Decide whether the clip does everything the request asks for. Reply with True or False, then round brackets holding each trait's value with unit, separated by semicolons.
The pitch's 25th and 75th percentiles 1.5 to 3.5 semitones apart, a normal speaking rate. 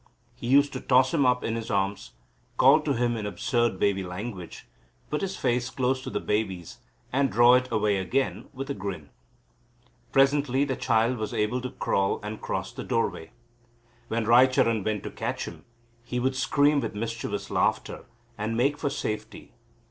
False (3.9 semitones; 175 wpm)